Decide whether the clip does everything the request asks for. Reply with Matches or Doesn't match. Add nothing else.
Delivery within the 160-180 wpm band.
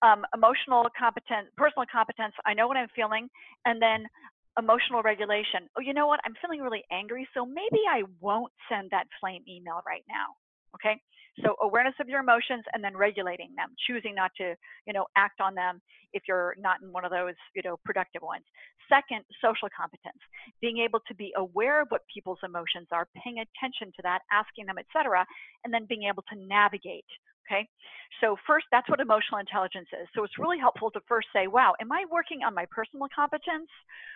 Doesn't match